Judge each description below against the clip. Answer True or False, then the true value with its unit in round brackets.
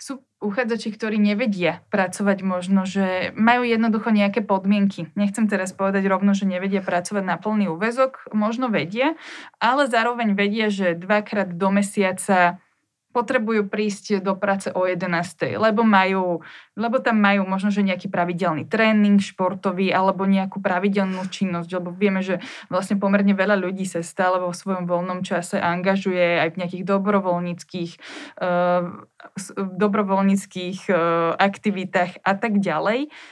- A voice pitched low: False (195 Hz)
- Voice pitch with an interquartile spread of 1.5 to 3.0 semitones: True (2.4 semitones)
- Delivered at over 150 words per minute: False (135 wpm)